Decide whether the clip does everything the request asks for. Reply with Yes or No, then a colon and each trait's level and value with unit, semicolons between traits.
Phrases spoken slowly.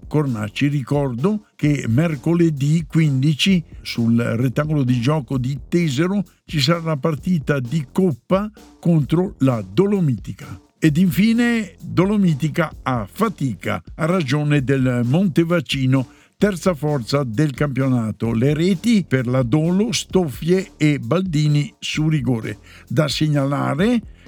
Yes: slow, 110 wpm